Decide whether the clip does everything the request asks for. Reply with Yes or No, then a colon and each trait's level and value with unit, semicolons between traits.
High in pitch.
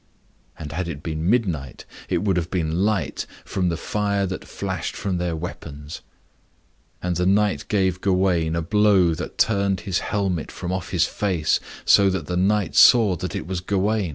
No: very low, 90 Hz